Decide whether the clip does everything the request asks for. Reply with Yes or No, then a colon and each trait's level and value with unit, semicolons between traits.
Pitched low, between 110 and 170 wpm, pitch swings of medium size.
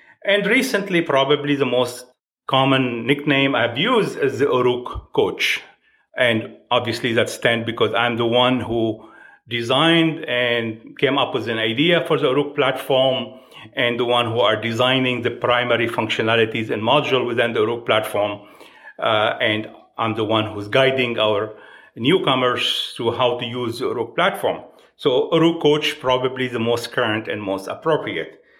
Yes: low, 125 Hz; average, 155 wpm; average, 3.8 semitones